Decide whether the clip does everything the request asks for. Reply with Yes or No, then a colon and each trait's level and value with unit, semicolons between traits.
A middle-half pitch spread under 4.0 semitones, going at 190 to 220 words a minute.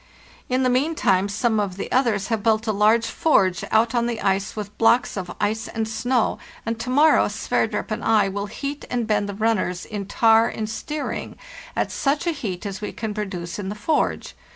Yes: average, 2.9 semitones; average, 200 wpm